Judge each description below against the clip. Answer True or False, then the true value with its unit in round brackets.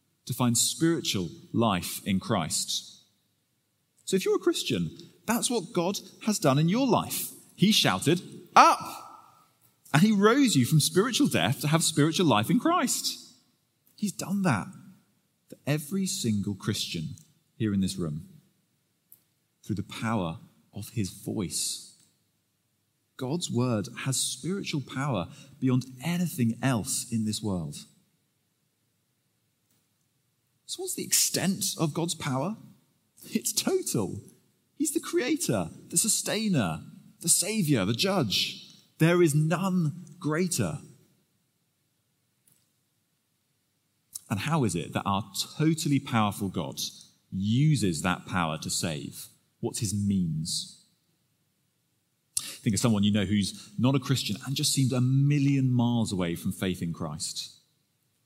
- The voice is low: False (145 Hz)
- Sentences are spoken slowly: True (125 wpm)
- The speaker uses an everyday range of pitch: False (7.4 semitones)